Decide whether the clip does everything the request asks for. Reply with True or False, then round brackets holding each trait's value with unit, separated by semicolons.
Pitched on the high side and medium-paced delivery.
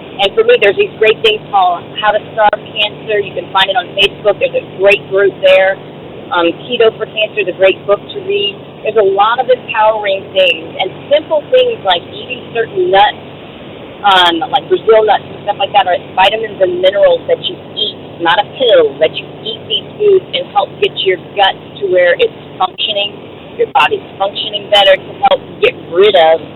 True (225 Hz; 195 wpm)